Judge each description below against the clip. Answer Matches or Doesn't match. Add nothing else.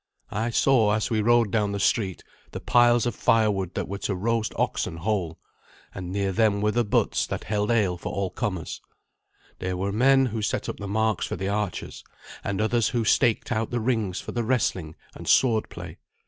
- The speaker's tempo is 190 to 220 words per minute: Matches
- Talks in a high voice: Doesn't match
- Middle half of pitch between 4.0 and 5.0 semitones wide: Doesn't match